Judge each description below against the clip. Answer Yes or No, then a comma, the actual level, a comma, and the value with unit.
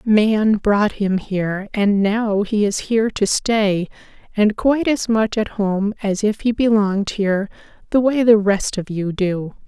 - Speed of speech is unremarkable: Yes, average, 180 wpm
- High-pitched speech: Yes, high, 210 Hz